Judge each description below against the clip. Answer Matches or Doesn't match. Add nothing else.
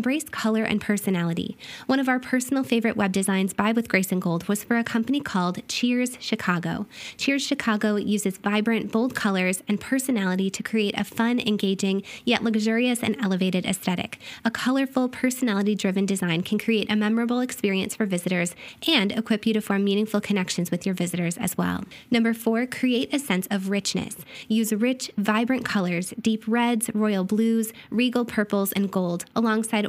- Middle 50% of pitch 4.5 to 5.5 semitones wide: Doesn't match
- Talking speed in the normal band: Matches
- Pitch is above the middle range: Matches